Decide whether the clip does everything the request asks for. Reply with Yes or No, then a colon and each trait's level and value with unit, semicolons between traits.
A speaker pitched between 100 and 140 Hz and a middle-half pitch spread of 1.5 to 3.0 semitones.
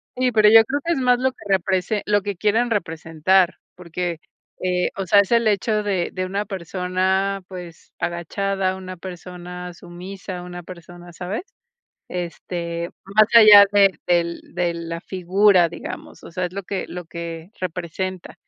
No: medium, 185 Hz; narrow, 2.6 semitones